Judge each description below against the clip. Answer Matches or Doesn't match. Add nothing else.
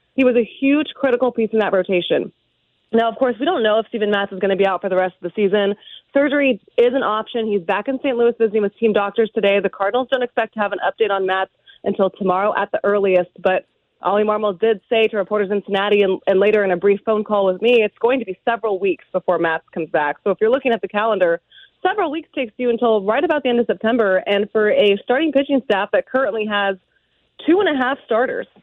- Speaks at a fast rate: Matches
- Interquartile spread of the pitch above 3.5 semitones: Matches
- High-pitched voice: Matches